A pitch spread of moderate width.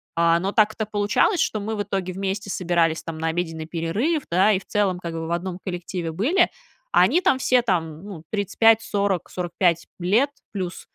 Yes: average, 3.7 semitones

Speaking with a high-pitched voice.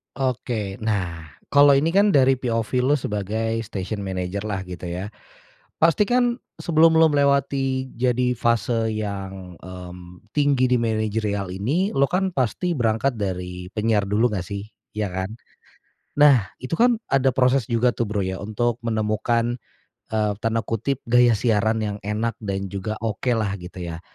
No: low, 110 Hz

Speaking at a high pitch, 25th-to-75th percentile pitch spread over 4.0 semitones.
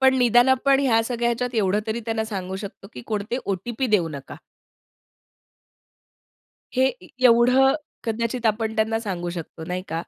No: high, 225 Hz; average, 3.7 semitones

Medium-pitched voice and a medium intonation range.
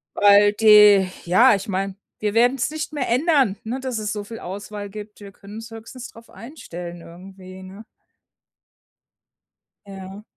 No: high, 210 Hz; average, 3.0 semitones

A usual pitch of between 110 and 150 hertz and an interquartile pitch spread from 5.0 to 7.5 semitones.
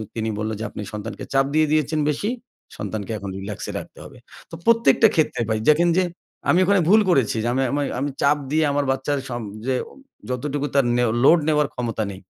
Yes: medium, 140 Hz; average, 5.3 semitones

